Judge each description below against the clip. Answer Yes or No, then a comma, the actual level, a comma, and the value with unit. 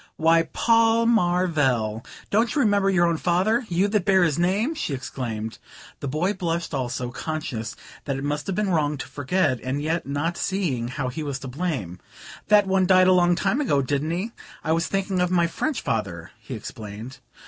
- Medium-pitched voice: Yes, medium, 165 Hz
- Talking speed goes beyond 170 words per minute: Yes, average, 195 wpm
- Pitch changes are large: Yes, wide, 5.9 semitones